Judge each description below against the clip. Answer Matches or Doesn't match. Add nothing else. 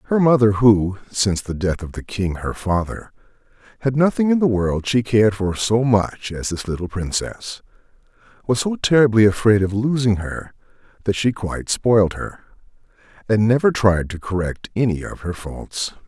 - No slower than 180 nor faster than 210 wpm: Doesn't match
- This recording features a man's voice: Matches